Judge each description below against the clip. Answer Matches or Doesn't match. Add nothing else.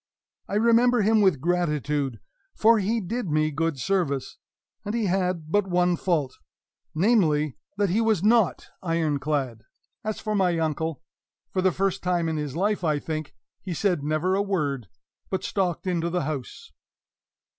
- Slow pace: Doesn't match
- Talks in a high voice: Doesn't match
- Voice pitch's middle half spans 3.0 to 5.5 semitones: Matches